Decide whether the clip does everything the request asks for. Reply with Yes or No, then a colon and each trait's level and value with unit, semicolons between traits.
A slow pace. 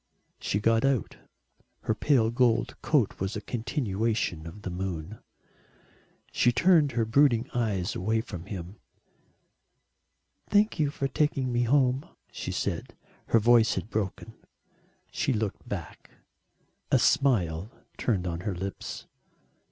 Yes: slow, 130 wpm